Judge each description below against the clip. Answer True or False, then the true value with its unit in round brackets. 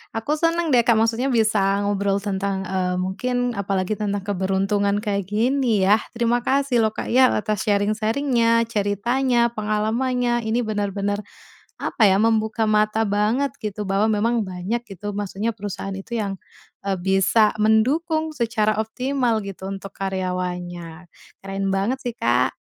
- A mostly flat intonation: False (3.2 semitones)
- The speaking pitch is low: False (215 Hz)